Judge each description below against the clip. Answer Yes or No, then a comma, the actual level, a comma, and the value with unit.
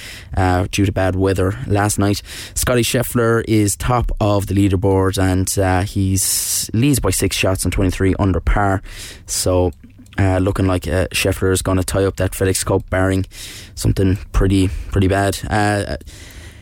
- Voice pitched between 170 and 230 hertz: No, very low, 95 Hz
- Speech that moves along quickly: No, average, 165 wpm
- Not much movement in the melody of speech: Yes, narrow, 1.7 semitones